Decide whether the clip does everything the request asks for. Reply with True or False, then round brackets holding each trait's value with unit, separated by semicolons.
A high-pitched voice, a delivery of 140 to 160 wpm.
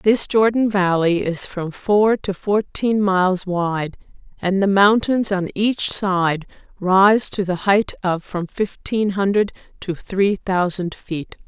True (195 Hz; 145 wpm)